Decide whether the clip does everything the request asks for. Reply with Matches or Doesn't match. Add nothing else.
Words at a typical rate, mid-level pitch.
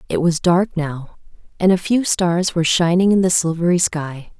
Matches